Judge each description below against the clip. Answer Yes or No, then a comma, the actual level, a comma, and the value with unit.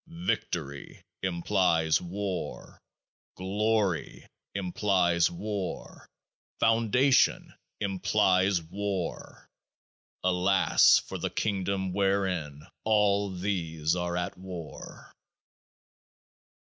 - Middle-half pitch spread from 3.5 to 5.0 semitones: No, average, 2.7 semitones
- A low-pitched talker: Yes, very low, 95 Hz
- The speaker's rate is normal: No, slow, 70 wpm